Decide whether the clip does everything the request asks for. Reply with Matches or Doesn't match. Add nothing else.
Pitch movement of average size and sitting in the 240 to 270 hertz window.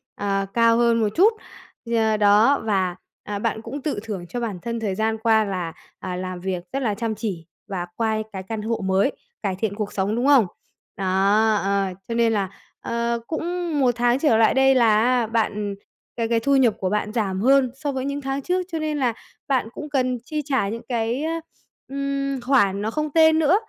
Doesn't match